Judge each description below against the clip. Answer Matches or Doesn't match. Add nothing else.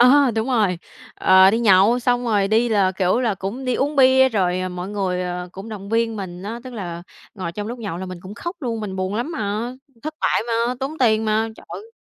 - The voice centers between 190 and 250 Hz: Matches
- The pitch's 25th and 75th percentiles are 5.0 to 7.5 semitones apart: Doesn't match